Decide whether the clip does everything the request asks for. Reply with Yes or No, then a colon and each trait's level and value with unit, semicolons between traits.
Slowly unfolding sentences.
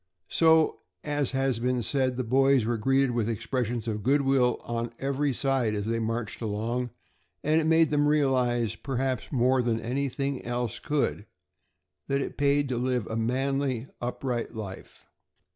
No: average, 160 wpm